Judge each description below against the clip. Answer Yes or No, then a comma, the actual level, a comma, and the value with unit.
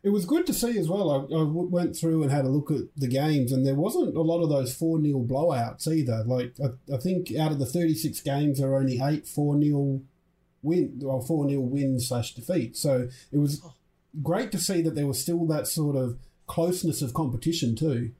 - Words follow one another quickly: Yes, fast, 220 wpm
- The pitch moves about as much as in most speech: Yes, average, 3.6 semitones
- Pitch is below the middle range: No, medium, 145 Hz